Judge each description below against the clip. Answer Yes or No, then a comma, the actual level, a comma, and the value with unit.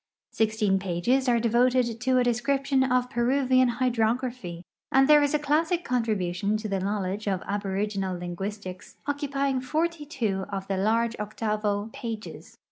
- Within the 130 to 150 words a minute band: Yes, average, 140 wpm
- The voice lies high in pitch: Yes, high, 230 Hz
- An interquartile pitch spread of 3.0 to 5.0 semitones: Yes, average, 4.4 semitones